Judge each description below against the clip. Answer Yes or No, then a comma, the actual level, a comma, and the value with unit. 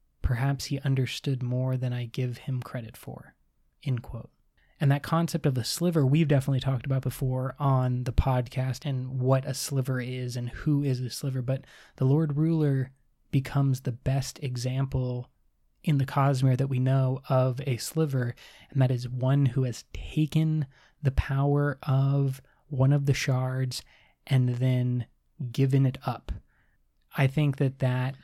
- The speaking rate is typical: Yes, average, 160 wpm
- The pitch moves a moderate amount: No, narrow, 1.6 semitones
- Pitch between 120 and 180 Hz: Yes, low, 130 Hz